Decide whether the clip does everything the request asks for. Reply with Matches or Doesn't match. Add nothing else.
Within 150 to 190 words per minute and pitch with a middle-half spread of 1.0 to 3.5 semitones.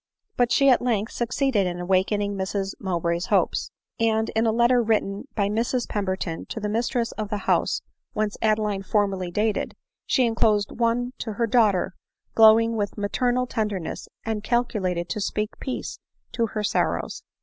Matches